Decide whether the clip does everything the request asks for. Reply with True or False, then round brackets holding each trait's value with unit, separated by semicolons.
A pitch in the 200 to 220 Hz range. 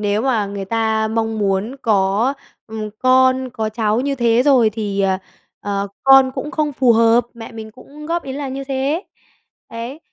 False (230 Hz)